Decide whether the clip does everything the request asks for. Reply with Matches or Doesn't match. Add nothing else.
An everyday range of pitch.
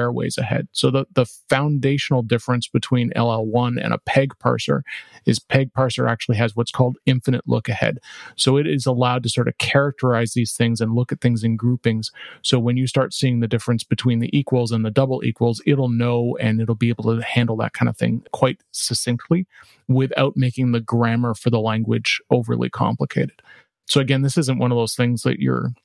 Doesn't match